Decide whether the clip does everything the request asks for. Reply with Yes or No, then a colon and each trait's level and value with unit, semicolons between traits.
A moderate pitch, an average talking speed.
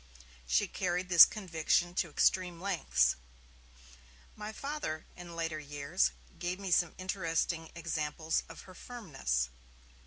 No: medium, 170 Hz; slow, 120 wpm